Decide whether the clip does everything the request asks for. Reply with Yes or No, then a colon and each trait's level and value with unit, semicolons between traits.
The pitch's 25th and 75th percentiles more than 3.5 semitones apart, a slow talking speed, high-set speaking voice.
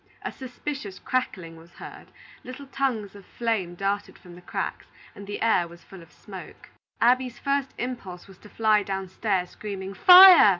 No: average, 5.2 semitones; average, 165 wpm; high, 205 Hz